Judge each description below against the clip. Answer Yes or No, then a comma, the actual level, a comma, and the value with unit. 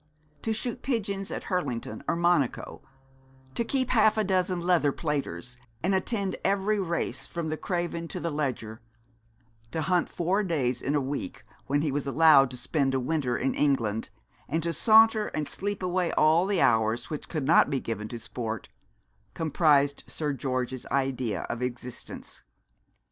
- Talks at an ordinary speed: Yes, average, 160 wpm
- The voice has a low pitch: No, medium, 155 Hz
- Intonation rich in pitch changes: Yes, wide, 5.9 semitones